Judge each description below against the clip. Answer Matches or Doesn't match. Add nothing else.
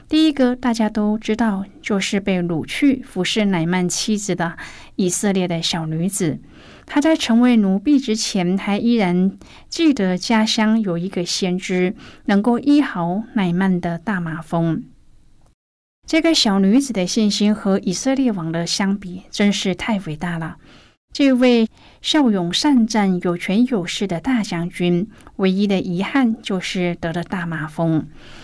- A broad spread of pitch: Doesn't match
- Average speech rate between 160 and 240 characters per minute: Matches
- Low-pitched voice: Doesn't match